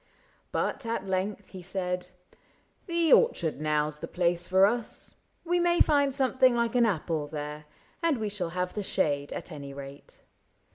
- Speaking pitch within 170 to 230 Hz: Yes, medium, 185 Hz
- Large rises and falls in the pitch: Yes, wide, 7.7 semitones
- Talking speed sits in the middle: Yes, average, 180 wpm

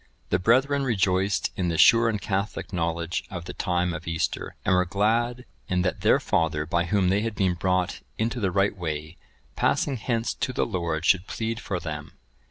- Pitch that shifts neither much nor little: Yes, average, 4.5 semitones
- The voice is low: Yes, very low, 95 Hz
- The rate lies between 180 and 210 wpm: Yes, average, 190 wpm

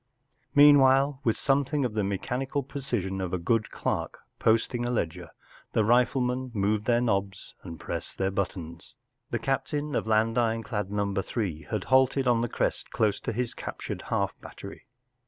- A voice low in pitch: Yes, low, 115 Hz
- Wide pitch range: No, average, 4.7 semitones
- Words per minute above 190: No, average, 165 wpm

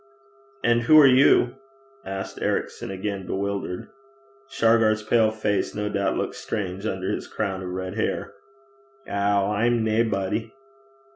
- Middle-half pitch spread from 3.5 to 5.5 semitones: No, average, 2.7 semitones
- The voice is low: Yes, low, 105 Hz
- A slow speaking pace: Yes, slow, 130 wpm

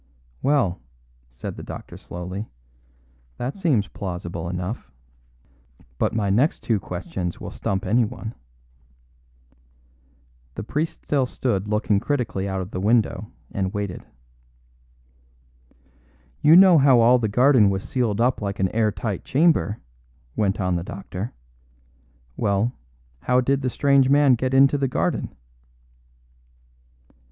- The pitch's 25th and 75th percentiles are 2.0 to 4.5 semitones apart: No, average, 5.2 semitones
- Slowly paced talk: Yes, slow, 125 wpm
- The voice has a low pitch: Yes, low, 110 Hz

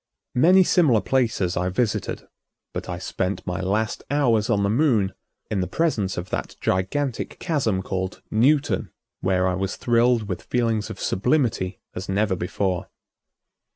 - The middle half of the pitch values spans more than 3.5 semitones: Yes, average, 4.9 semitones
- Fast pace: No, average, 150 wpm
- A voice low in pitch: Yes, low, 105 Hz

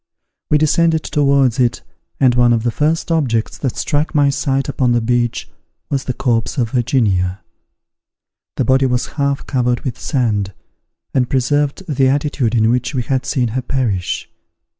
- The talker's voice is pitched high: No, low, 130 Hz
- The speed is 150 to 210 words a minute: Yes, average, 160 wpm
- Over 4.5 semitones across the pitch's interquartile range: No, average, 2.8 semitones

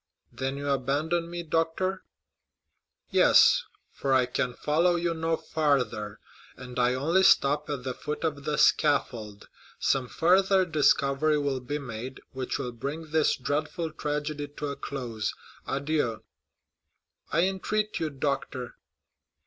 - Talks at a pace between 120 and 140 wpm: Yes, slow, 135 wpm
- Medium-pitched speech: Yes, medium, 145 Hz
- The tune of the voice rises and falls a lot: No, average, 3.7 semitones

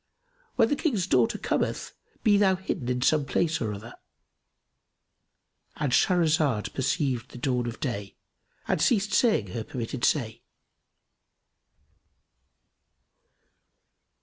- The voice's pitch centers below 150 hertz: Yes, low, 135 Hz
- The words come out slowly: Yes, slow, 105 wpm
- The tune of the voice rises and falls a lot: Yes, wide, 7.5 semitones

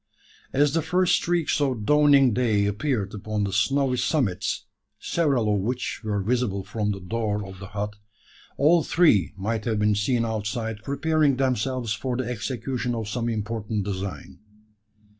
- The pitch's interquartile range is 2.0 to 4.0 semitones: No, average, 4.4 semitones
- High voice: No, low, 115 Hz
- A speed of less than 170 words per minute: Yes, average, 155 wpm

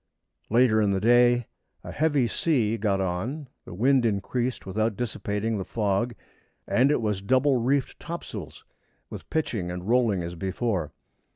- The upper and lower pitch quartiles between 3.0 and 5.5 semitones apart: Yes, average, 4.2 semitones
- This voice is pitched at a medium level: No, low, 115 Hz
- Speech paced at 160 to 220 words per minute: No, average, 150 wpm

